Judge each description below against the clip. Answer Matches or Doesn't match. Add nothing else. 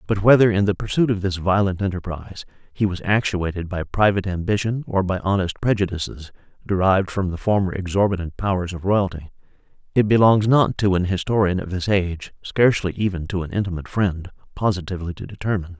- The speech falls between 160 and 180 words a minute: Matches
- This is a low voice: Matches